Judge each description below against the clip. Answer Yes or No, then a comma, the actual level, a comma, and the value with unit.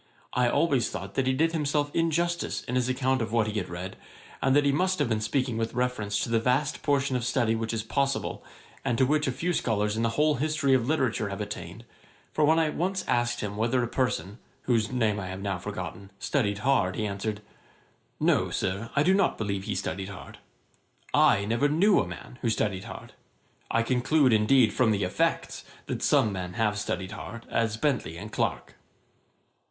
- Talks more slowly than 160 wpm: No, average, 200 wpm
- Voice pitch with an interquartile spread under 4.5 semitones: No, average, 5.0 semitones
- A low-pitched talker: Yes, low, 120 Hz